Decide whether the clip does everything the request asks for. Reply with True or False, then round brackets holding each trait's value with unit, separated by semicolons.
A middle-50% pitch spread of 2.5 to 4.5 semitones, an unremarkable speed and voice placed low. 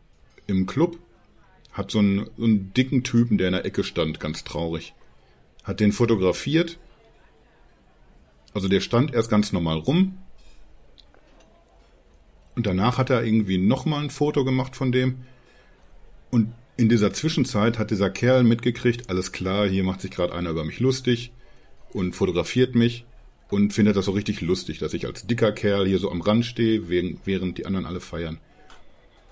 False (4.9 semitones; 160 wpm; 105 Hz)